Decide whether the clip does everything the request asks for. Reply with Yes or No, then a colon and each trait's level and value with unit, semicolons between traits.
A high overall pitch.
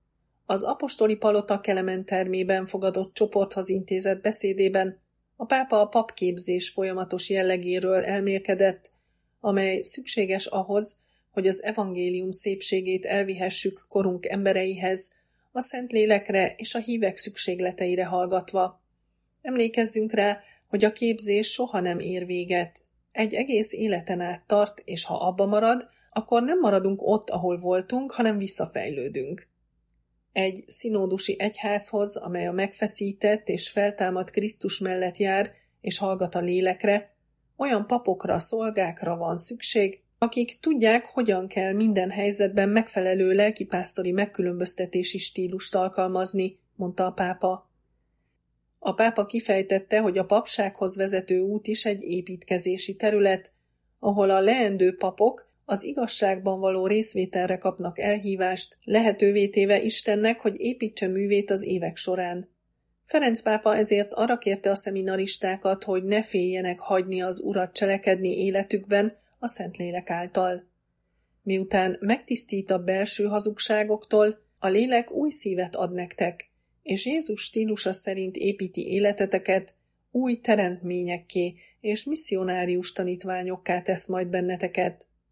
Yes: high, 195 Hz